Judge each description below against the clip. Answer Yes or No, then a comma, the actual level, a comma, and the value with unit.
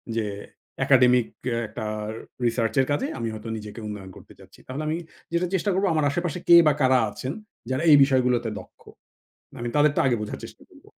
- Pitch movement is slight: No, average, 4.5 semitones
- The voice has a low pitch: Yes, low, 130 Hz